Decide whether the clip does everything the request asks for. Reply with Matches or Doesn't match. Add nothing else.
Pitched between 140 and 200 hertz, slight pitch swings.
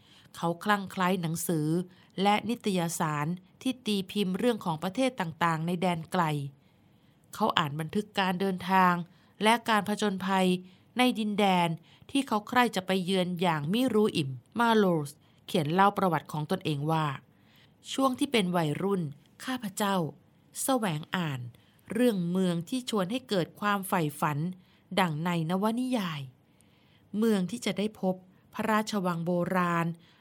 Doesn't match